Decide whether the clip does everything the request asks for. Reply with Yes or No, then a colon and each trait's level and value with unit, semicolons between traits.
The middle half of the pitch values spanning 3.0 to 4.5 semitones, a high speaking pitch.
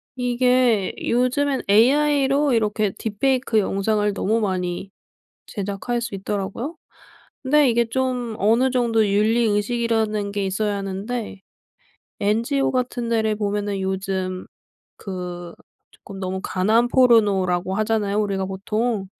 Yes: average, 3.6 semitones; high, 215 Hz